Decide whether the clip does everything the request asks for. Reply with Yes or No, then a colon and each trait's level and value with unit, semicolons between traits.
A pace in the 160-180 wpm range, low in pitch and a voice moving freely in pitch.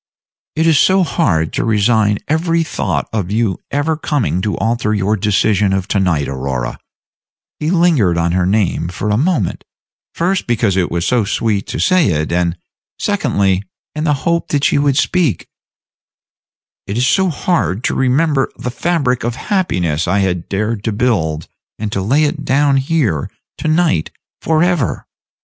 Yes: average, 165 wpm; low, 115 Hz; wide, 8.2 semitones